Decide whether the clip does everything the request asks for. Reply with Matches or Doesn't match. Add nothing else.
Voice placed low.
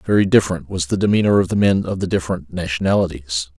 Matches